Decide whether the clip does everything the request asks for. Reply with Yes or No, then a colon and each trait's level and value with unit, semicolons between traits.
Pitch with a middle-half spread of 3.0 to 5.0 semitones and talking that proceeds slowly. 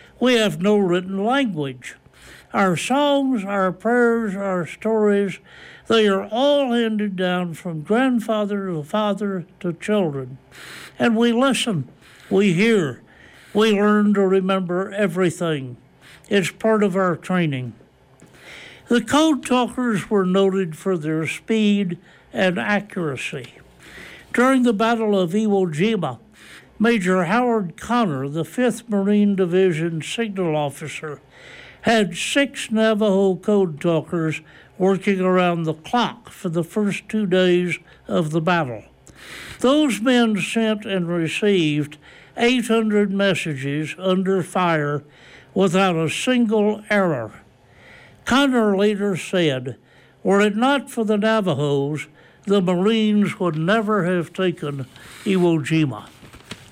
Yes: average, 4.5 semitones; slow, 115 wpm